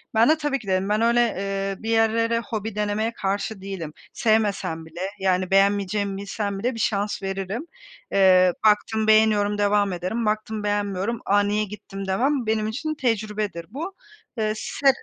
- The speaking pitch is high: Yes, high, 210 Hz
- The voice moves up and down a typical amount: No, narrow, 2.2 semitones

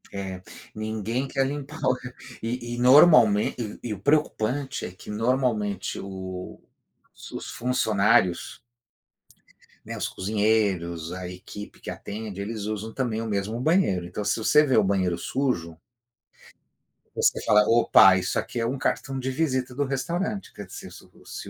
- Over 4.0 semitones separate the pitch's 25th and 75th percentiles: Yes, average, 4.8 semitones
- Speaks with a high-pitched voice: No, low, 110 Hz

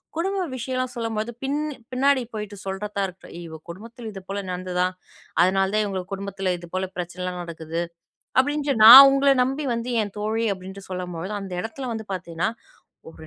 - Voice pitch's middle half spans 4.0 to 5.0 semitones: Yes, average, 4.7 semitones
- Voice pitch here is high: Yes, high, 200 Hz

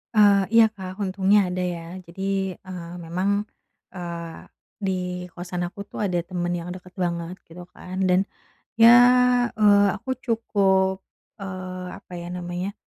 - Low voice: No, medium, 185 Hz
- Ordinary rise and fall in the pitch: No, narrow, 2.0 semitones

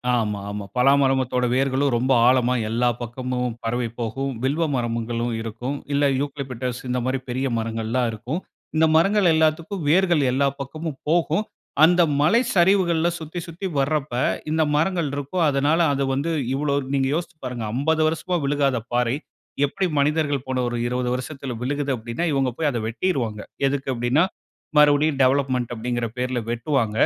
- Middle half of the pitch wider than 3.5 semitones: Yes, average, 4.1 semitones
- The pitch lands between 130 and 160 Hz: Yes, low, 135 Hz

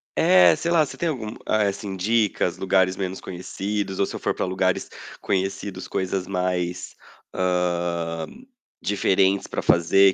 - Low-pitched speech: Yes, very low, 95 Hz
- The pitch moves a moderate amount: No, narrow, 1.8 semitones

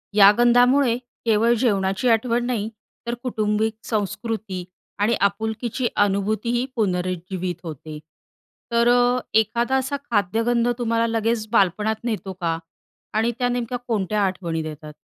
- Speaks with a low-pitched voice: No, high, 220 Hz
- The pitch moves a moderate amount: Yes, average, 3.5 semitones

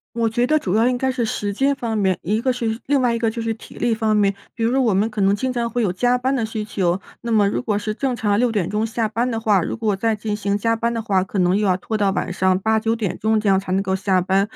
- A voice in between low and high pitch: No, high, 220 Hz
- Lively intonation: No, average, 2.7 semitones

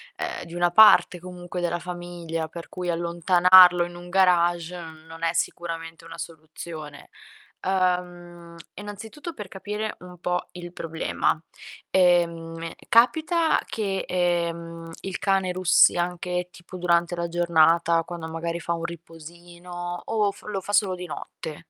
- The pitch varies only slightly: Yes, narrow, 1.4 semitones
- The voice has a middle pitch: Yes, medium, 175 Hz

